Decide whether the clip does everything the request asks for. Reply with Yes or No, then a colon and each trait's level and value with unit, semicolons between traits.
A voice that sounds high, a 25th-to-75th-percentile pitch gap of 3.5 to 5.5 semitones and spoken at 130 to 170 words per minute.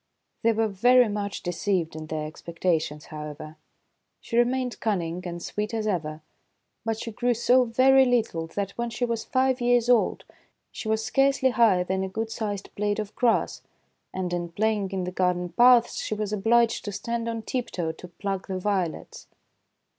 No: high, 210 Hz; average, 4.7 semitones; average, 180 wpm